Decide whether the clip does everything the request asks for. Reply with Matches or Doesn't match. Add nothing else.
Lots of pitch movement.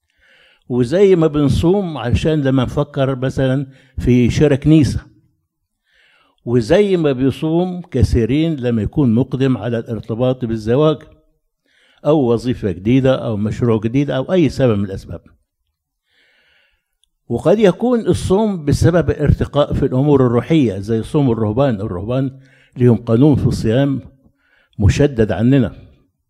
Doesn't match